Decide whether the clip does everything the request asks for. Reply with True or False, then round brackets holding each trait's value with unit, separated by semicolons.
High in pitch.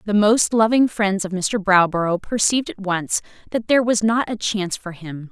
True (200 Hz)